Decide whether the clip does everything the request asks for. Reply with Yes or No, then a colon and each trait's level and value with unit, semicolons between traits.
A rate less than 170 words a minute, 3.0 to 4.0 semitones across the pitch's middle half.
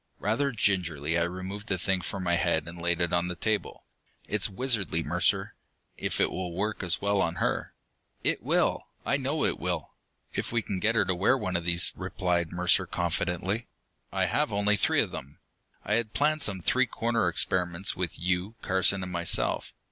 No: average, 190 wpm; average, 3.4 semitones